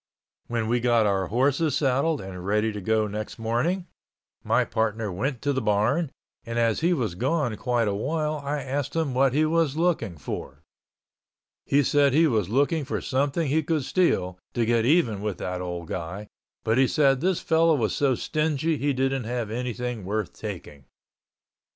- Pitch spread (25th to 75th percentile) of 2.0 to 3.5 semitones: No, average, 5.2 semitones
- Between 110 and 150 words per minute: No, average, 180 wpm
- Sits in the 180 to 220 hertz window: No, low, 125 Hz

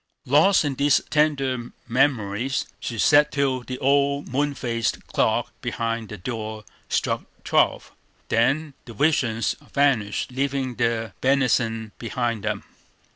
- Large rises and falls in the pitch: No, average, 3.5 semitones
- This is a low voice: Yes, low, 130 Hz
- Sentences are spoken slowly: Yes, slow, 125 wpm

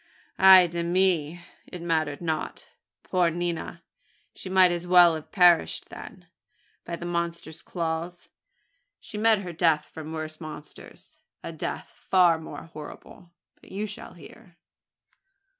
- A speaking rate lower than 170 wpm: Yes, slow, 135 wpm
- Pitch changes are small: Yes, narrow, 1.9 semitones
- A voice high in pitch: No, medium, 170 Hz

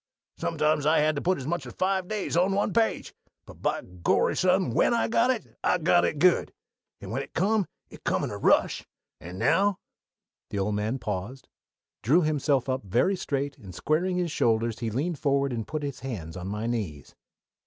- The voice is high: No, medium, 145 Hz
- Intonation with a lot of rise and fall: Yes, wide, 8.1 semitones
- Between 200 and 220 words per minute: Yes, fast, 205 wpm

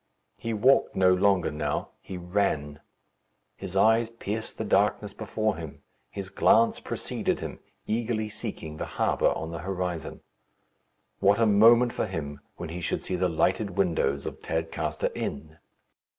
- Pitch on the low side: Yes, very low, 95 Hz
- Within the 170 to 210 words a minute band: No, average, 150 wpm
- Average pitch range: Yes, average, 5.0 semitones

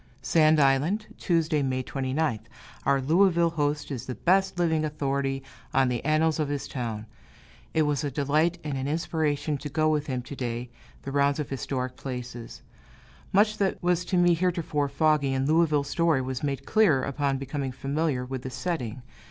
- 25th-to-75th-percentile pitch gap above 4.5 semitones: No, average, 3.2 semitones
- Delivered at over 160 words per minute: Yes, average, 175 wpm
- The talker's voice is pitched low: No, medium, 145 Hz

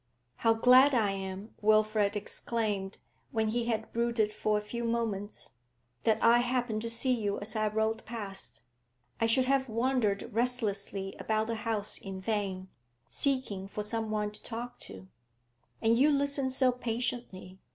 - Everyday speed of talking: Yes, average, 155 wpm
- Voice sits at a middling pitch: No, high, 220 Hz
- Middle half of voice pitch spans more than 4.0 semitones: No, narrow, 2.6 semitones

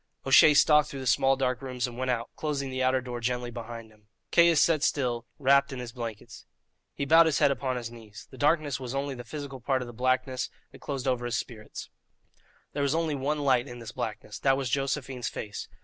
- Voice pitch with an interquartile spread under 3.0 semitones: Yes, narrow, 2.5 semitones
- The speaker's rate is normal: No, fast, 220 wpm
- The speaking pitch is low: Yes, low, 130 Hz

